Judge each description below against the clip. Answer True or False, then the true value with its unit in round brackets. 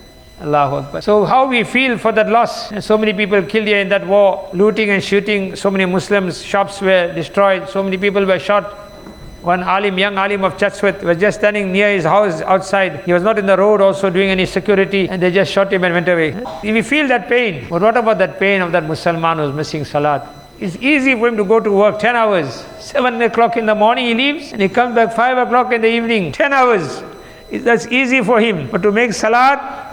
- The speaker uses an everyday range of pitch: True (3.1 semitones)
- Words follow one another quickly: True (230 wpm)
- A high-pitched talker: True (205 Hz)